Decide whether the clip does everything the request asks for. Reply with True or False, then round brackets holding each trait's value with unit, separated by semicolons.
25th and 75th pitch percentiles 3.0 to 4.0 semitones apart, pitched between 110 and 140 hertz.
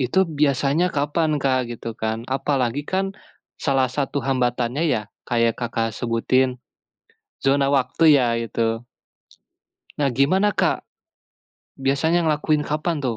True (3.7 semitones; 135 Hz)